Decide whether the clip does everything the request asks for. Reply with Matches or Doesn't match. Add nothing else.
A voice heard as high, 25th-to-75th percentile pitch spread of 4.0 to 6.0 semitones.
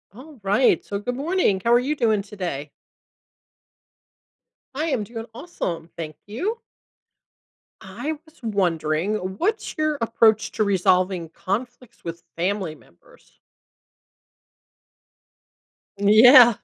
Matches